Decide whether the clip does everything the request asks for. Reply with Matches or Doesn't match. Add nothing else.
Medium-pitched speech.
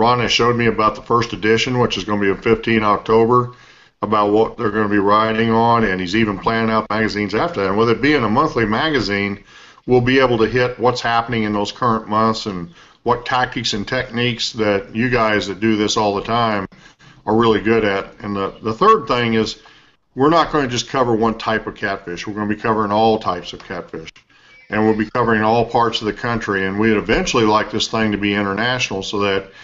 Doesn't match